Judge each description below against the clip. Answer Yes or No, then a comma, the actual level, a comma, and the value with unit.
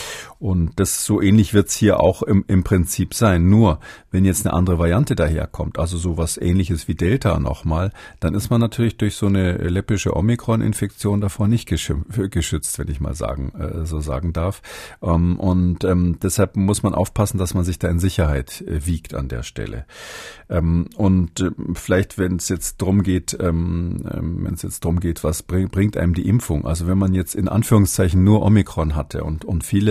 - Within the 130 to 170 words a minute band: No, average, 180 wpm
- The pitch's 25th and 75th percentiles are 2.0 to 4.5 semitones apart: Yes, average, 3.1 semitones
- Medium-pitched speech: No, very low, 90 Hz